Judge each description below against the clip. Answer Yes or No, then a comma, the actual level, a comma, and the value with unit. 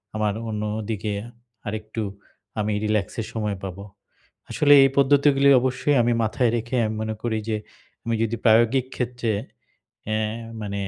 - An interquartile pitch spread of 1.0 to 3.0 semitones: Yes, narrow, 2.5 semitones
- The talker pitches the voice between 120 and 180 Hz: No, low, 110 Hz